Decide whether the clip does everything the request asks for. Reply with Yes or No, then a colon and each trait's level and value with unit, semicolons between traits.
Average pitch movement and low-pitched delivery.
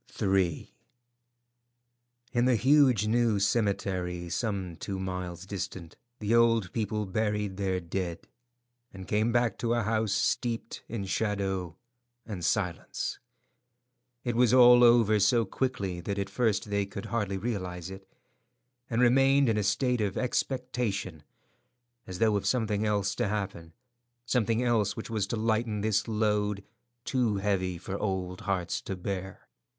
Yes: average, 3.2 semitones; low, 105 Hz